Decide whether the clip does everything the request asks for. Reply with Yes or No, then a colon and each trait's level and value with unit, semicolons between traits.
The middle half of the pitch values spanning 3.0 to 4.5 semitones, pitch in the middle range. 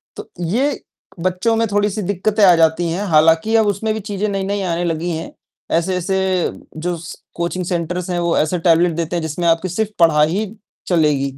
Yes: average, 3.3 semitones; medium, 180 Hz